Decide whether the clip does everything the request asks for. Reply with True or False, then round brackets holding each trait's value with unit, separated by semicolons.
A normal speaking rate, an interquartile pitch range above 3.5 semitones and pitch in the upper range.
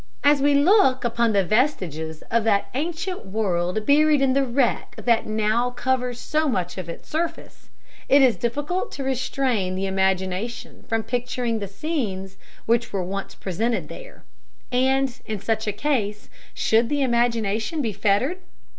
True (155 wpm; 5.2 semitones; 235 Hz)